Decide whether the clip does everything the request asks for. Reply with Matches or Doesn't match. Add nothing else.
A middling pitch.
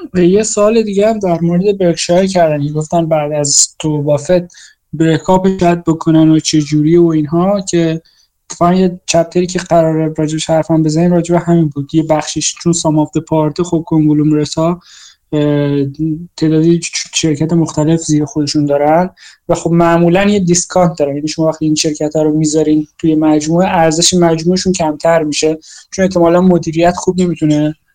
Matches